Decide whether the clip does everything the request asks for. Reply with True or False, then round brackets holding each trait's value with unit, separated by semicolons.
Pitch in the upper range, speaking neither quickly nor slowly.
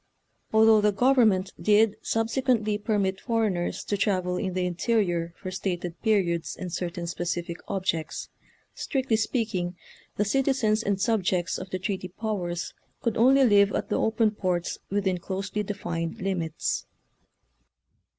False (195 Hz; 130 wpm)